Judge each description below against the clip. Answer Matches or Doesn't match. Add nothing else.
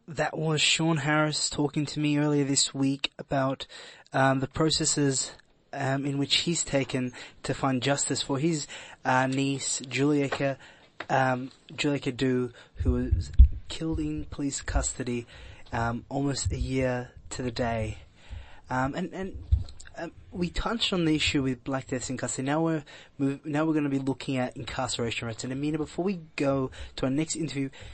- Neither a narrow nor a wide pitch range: Matches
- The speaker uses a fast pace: Doesn't match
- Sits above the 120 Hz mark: Matches